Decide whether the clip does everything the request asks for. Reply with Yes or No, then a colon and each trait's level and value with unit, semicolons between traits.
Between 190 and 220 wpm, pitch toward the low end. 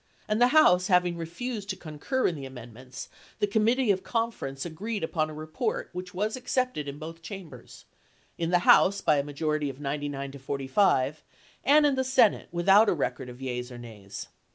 No: average, 200 wpm; medium, 165 Hz